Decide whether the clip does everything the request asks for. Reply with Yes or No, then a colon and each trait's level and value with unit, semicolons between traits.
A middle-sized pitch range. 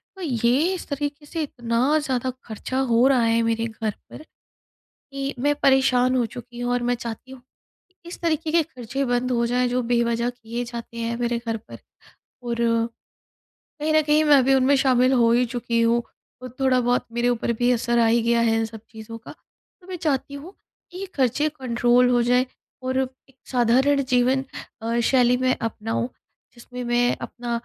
No: narrow, 2.2 semitones